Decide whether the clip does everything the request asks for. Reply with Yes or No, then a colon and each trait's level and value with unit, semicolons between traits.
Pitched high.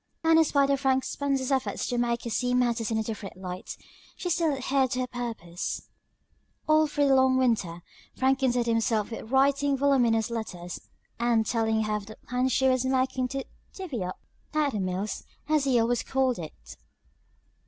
Yes: very high, 250 Hz